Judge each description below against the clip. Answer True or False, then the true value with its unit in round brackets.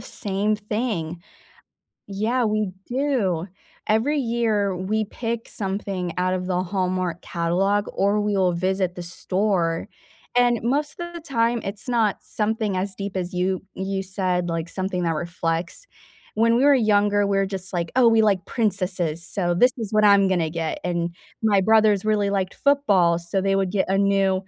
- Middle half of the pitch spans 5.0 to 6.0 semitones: False (3.0 semitones)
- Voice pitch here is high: True (195 Hz)